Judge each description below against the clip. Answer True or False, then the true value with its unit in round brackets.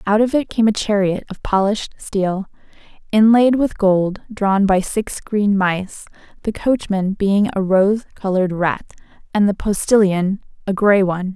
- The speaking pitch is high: True (200 Hz)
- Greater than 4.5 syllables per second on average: False (4.4 syllables/s)